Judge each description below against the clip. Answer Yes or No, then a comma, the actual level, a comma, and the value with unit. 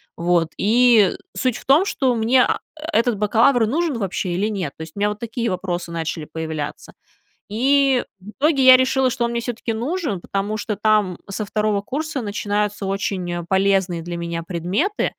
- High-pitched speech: Yes, high, 210 Hz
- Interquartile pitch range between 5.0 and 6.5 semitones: Yes, average, 5.3 semitones